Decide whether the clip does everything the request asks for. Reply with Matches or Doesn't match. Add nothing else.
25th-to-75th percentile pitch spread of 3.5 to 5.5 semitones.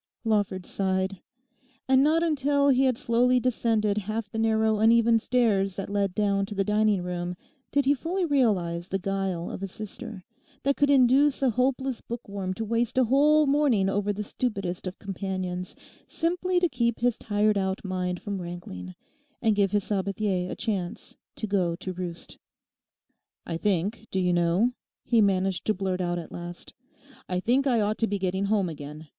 Matches